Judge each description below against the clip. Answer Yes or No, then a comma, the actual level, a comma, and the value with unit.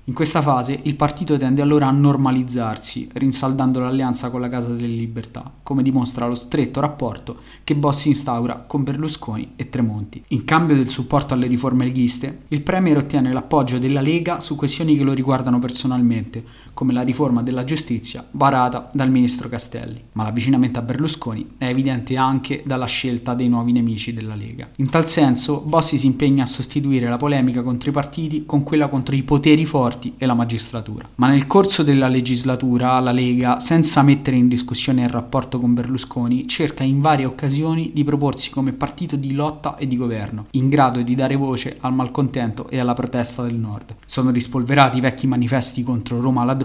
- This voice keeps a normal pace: No, fast, 180 wpm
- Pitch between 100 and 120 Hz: No, low, 130 Hz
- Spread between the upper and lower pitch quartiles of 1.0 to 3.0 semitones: Yes, narrow, 2.5 semitones